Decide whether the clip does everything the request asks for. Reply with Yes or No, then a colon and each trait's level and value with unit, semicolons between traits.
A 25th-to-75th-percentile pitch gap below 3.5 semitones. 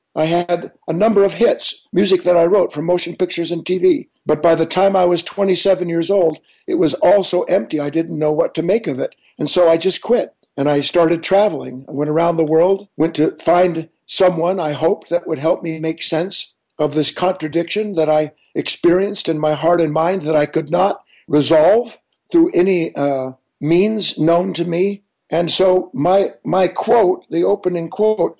Yes: average, 3.0 semitones